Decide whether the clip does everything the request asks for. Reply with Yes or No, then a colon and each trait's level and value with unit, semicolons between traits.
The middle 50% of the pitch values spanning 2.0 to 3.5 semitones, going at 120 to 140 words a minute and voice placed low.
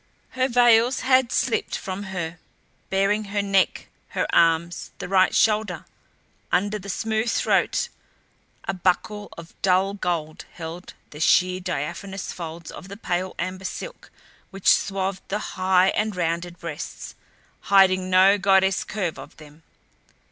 No: narrow, 2.5 semitones; slow, 135 wpm; high, 190 Hz